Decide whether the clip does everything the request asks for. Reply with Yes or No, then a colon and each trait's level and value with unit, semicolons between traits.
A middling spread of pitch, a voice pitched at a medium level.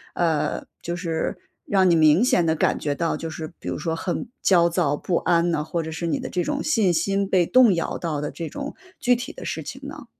Yes: average, 3.3 semitones; medium, 170 Hz